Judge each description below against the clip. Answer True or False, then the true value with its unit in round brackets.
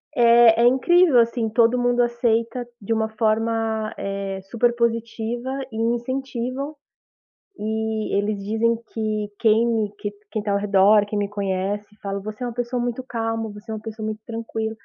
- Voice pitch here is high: True (225 Hz)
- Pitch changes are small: True (1.9 semitones)